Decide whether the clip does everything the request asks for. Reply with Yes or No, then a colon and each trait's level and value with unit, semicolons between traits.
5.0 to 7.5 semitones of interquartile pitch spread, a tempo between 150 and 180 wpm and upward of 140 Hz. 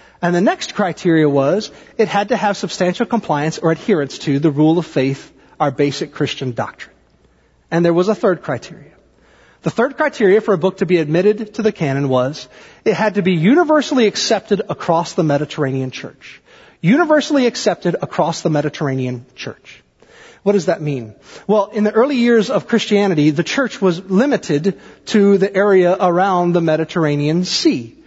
Yes: wide, 5.5 semitones; average, 170 wpm; medium, 185 Hz